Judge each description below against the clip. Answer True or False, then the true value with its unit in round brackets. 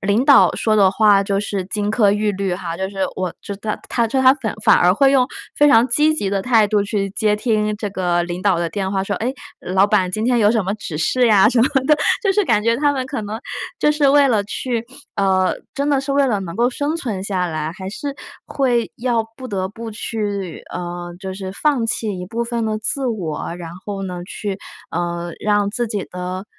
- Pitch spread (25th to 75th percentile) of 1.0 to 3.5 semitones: False (4.0 semitones)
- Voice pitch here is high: True (210 Hz)